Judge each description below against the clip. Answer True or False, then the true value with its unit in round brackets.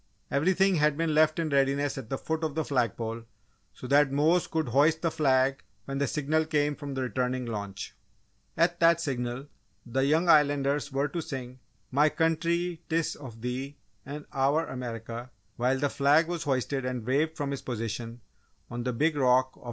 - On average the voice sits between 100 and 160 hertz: True (140 Hz)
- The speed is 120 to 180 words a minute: False (190 wpm)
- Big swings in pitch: False (3.7 semitones)